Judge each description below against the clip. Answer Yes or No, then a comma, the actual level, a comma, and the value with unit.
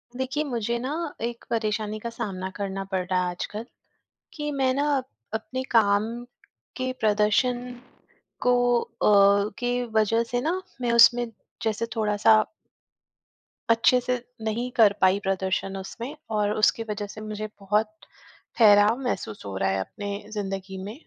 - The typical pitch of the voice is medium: No, high, 215 Hz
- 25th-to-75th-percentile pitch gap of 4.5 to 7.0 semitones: No, average, 3.2 semitones